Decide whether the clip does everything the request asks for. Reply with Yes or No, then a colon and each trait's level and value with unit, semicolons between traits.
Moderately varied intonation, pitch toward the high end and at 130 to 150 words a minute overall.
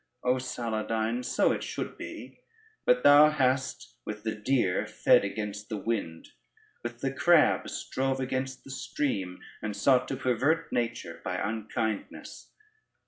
No: average, 3.9 semitones; low, 120 Hz; average, 140 wpm